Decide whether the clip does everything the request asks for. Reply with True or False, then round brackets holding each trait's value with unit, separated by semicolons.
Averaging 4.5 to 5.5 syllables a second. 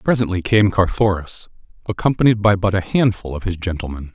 False (5.7 syllables/s)